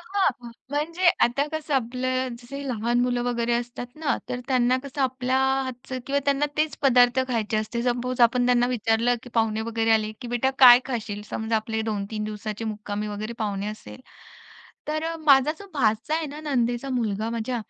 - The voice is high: Yes, high, 245 Hz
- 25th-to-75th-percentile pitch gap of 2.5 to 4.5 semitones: Yes, average, 2.8 semitones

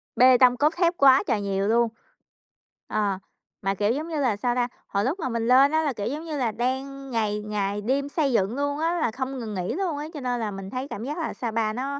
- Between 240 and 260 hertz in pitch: Yes, very high, 250 Hz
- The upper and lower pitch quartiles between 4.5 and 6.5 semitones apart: Yes, average, 4.8 semitones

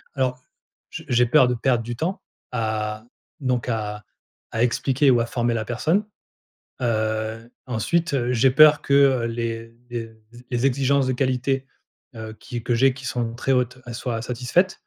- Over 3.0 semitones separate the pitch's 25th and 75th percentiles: No, narrow, 2.5 semitones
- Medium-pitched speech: No, low, 125 Hz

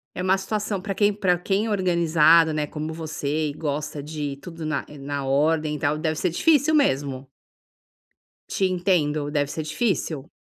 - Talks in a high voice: No, medium, 160 Hz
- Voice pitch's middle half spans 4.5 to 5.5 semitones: No, average, 4.0 semitones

